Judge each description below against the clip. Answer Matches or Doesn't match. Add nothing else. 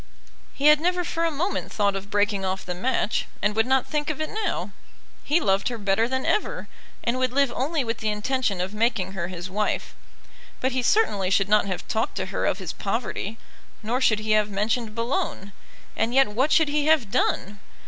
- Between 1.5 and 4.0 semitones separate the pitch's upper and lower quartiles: Doesn't match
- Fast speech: Matches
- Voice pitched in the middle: Doesn't match